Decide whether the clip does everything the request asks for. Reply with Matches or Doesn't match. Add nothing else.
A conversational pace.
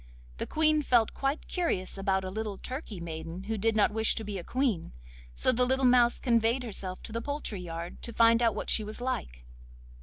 Doesn't match